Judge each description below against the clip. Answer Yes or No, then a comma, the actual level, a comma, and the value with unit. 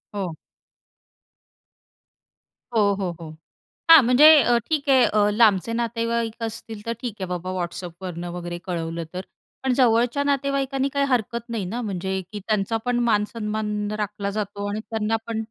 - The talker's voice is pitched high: Yes, high, 215 Hz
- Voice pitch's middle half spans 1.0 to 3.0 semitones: No, average, 3.7 semitones